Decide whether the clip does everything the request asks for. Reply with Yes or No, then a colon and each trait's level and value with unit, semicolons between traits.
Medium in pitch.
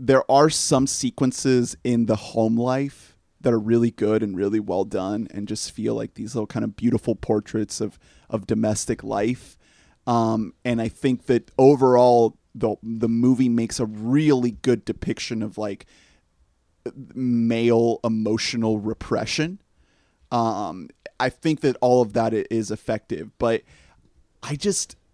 No: low, 115 Hz